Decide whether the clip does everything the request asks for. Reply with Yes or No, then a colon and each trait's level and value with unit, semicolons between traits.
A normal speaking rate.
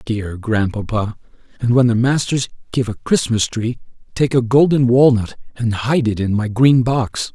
Yes: average, 170 wpm